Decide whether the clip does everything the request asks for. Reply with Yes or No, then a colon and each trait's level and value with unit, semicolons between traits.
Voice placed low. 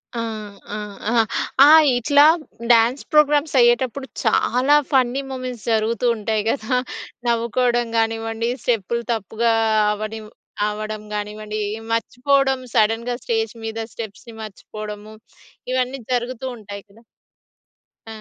No: high, 230 Hz